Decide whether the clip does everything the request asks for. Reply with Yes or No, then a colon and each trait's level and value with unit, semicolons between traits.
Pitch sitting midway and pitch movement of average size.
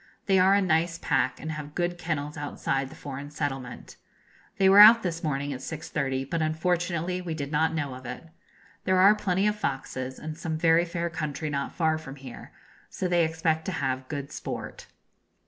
Yes: medium, 160 Hz; average, 3.7 semitones